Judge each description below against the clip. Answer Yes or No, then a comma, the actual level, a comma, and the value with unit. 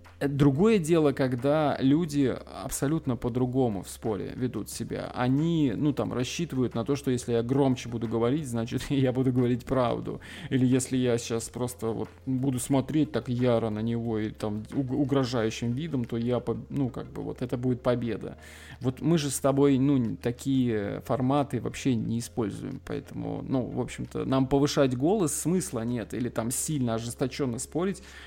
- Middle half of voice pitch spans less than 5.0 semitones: Yes, average, 3.1 semitones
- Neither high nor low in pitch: No, low, 130 Hz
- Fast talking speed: Yes, fast, 165 wpm